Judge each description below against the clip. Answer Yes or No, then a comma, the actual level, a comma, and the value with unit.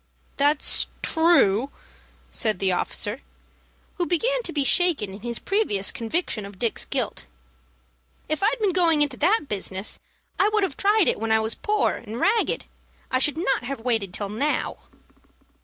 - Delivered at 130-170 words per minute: Yes, average, 160 wpm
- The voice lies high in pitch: Yes, very high, 275 Hz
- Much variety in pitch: Yes, wide, 8.5 semitones